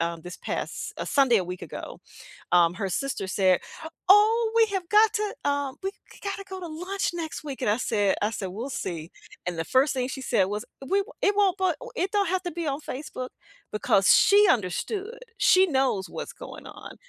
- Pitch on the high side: Yes, very high, 280 Hz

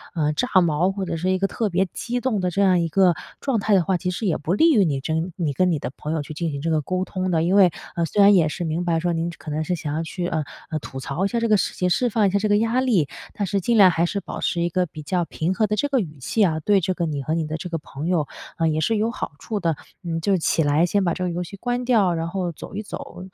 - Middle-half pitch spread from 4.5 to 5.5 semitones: No, average, 3.7 semitones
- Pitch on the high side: No, medium, 180 Hz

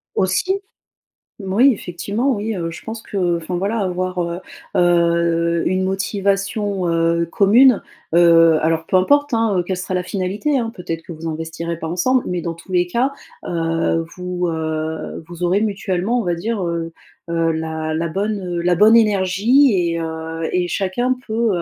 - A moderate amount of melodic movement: Yes, average, 3.5 semitones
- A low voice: No, medium, 180 Hz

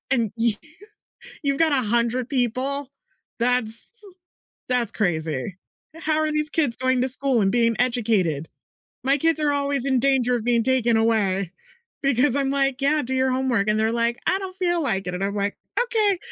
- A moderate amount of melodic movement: Yes, average, 3.9 semitones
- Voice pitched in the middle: No, very high, 250 Hz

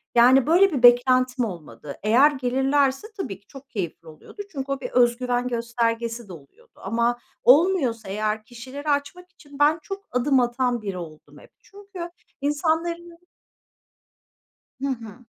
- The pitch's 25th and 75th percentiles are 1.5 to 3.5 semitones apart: No, average, 4.0 semitones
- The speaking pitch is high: Yes, very high, 250 Hz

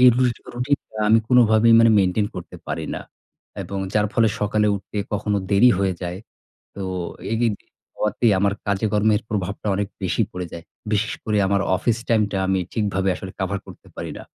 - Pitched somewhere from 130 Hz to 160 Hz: No, low, 105 Hz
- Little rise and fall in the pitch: Yes, narrow, 2.3 semitones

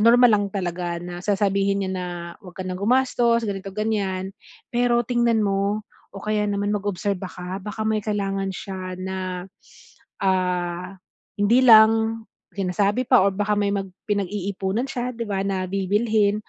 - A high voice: Yes, high, 200 Hz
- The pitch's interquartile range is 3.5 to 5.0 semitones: No, narrow, 2.5 semitones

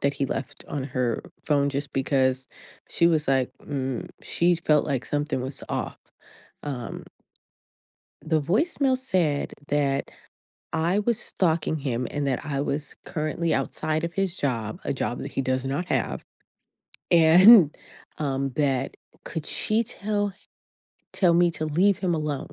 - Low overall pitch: No, medium, 150 Hz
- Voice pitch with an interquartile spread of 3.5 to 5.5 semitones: Yes, average, 4.0 semitones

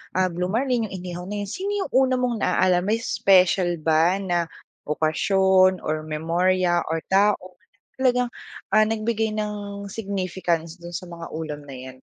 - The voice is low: No, medium, 185 Hz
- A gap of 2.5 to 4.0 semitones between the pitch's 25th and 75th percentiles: Yes, average, 3.7 semitones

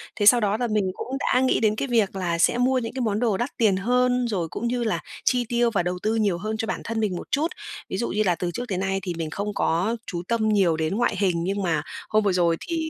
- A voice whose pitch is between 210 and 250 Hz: Yes, high, 215 Hz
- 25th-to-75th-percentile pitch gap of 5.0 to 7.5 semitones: No, average, 4.3 semitones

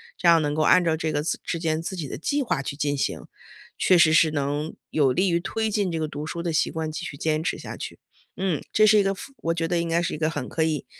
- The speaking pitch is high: No, medium, 160 Hz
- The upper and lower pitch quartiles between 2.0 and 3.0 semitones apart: Yes, narrow, 2.4 semitones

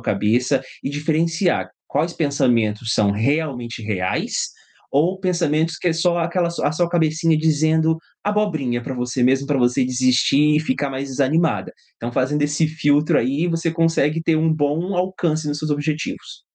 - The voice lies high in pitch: No, medium, 150 Hz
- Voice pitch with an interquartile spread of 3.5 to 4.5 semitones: Yes, average, 3.8 semitones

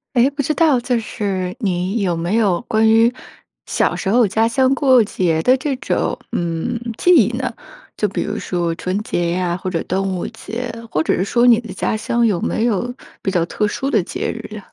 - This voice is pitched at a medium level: No, high, 215 Hz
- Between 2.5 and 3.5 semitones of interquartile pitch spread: No, average, 4.9 semitones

